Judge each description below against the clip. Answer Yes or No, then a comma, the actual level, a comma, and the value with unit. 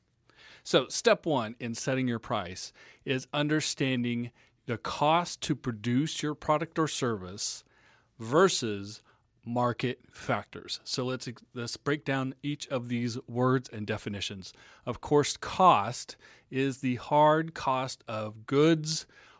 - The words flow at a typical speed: No, slow, 125 wpm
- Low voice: Yes, low, 130 Hz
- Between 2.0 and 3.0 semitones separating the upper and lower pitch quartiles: No, average, 3.8 semitones